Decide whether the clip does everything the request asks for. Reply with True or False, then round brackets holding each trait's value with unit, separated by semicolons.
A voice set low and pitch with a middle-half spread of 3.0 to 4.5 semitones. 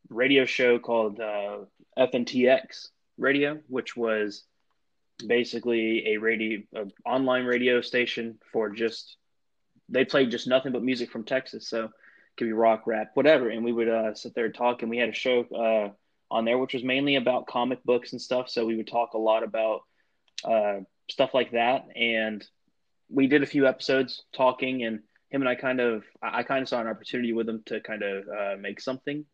False (120 Hz; 2.6 semitones)